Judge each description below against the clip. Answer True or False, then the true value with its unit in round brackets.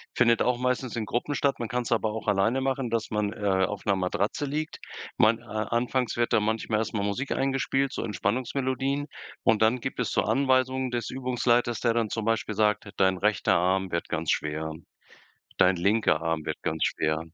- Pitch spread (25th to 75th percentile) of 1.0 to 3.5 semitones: False (4.0 semitones)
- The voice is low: True (115 Hz)